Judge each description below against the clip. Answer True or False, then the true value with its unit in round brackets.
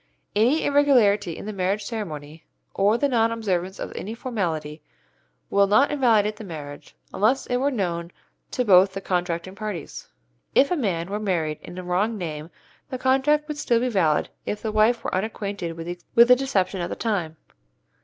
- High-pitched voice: True (205 Hz)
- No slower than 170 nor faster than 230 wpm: True (175 wpm)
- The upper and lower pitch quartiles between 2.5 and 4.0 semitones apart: False (5.1 semitones)